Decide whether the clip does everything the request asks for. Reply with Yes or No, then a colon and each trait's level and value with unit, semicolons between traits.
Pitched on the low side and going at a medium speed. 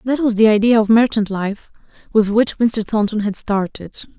No: high, 215 Hz; average, 185 wpm